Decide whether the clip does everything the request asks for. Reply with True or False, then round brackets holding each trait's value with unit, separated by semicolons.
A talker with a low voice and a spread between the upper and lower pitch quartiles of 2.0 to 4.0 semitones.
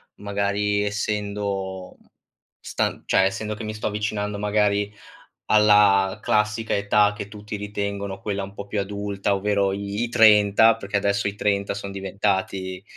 False (100 Hz; 0.9 semitones)